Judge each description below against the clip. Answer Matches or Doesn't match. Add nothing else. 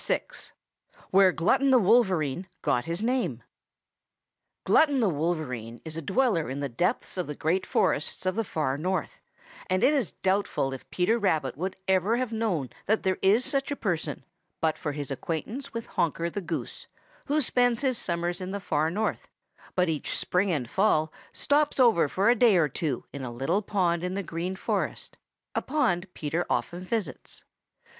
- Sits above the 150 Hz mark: Matches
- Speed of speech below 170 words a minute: Doesn't match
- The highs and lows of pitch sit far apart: Matches